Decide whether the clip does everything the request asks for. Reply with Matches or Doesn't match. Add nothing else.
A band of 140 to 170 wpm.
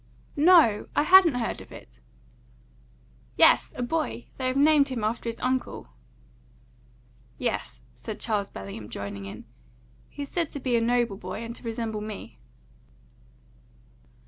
Matches